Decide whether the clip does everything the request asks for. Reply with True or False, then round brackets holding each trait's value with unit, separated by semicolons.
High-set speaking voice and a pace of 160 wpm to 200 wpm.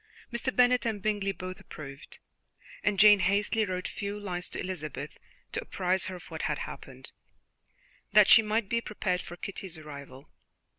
True (195 Hz; 165 wpm)